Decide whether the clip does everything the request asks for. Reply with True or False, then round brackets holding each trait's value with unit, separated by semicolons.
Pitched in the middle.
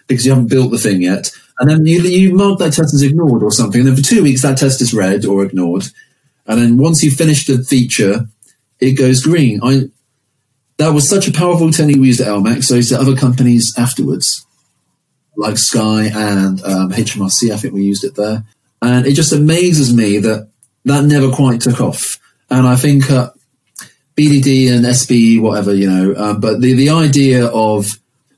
False (125 Hz)